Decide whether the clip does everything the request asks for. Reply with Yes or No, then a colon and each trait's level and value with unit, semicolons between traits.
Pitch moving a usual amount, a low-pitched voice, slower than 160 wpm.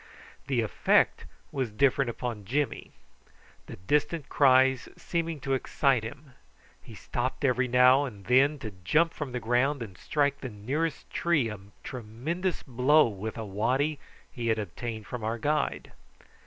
Yes: average, 4.1 semitones; low, 130 Hz; average, 150 wpm